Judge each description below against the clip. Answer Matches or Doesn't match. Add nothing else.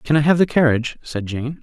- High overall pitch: Doesn't match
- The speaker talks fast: Matches